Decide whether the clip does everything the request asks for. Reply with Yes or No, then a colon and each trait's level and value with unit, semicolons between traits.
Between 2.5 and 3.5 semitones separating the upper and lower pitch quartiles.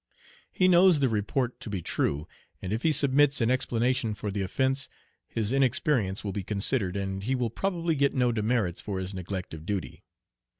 No: wide, 5.4 semitones